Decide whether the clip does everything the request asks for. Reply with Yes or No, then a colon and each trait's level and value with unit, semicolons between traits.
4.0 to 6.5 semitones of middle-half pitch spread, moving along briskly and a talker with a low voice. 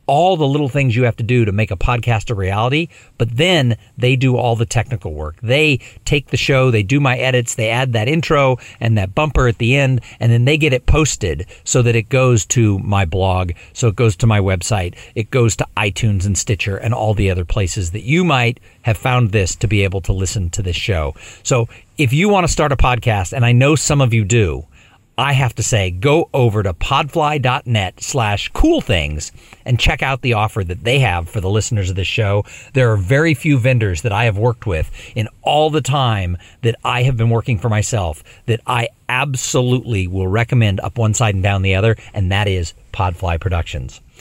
Yes: average, 4.3 semitones; fast, 220 wpm; low, 115 Hz